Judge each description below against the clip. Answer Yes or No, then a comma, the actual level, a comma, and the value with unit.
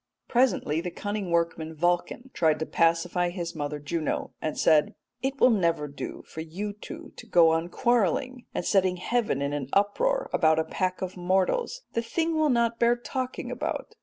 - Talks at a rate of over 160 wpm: Yes, average, 180 wpm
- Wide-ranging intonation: Yes, wide, 6.6 semitones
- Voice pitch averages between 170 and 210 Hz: Yes, medium, 185 Hz